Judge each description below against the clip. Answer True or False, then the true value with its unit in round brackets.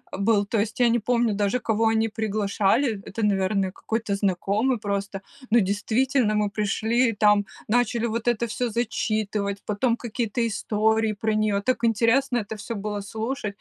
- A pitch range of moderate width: False (2.3 semitones)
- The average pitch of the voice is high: True (220 Hz)